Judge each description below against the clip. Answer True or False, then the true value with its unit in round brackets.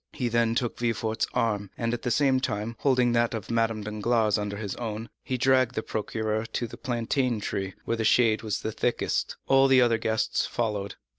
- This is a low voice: True (115 Hz)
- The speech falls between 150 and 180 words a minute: False (195 wpm)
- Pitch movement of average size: False (2.1 semitones)